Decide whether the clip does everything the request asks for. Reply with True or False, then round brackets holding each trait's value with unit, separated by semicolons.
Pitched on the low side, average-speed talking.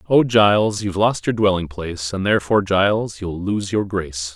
True (100 Hz; 195 wpm)